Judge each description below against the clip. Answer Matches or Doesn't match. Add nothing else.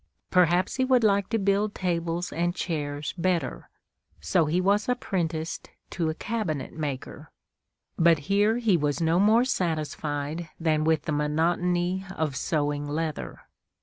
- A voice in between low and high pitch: Matches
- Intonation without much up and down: Doesn't match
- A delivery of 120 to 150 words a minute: Matches